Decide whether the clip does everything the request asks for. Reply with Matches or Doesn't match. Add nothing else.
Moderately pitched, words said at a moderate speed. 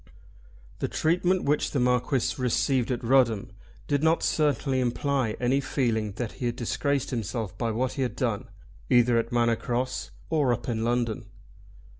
Doesn't match